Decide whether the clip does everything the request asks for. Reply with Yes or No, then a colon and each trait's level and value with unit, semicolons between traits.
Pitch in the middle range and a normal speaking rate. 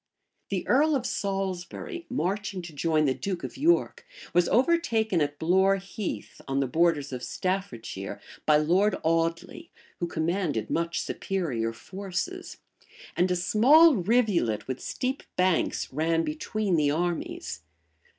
No: medium, 180 Hz; slow, 130 wpm